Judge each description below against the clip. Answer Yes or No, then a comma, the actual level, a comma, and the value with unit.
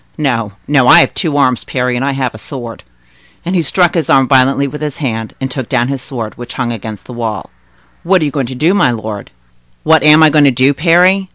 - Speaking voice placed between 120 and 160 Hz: Yes, low, 135 Hz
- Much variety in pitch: No, average, 3.9 semitones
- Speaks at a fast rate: Yes, fast, 245 wpm